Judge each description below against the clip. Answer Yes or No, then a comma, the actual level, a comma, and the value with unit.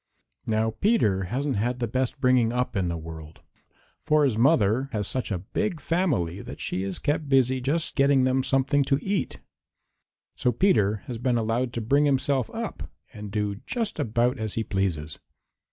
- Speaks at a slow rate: No, average, 175 wpm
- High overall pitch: No, low, 125 Hz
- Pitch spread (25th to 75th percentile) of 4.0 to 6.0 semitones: Yes, average, 4.9 semitones